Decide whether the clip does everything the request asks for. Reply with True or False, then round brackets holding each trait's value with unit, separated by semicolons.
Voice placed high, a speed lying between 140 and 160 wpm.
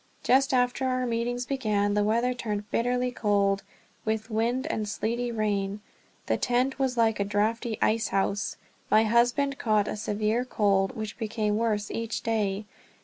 True (220 Hz; 155 wpm)